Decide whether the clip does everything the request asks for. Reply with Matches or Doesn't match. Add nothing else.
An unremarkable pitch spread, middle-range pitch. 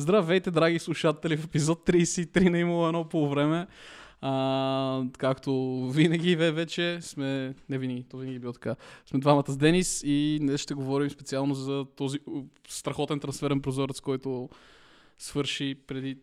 Matches